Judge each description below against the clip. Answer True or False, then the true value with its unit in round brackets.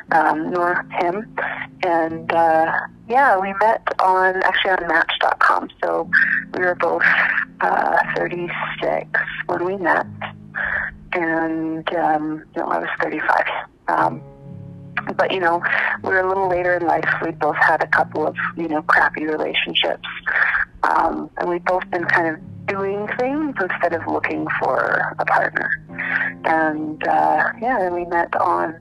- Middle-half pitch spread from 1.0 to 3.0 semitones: True (2.7 semitones)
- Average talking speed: True (150 wpm)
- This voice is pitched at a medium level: True (175 Hz)